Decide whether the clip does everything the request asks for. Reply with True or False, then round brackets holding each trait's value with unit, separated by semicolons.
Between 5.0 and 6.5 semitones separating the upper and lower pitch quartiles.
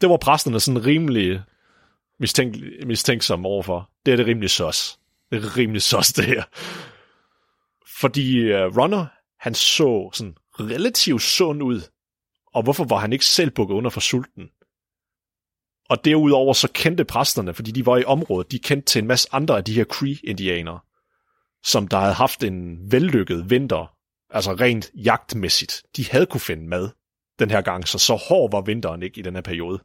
True (5.5 semitones)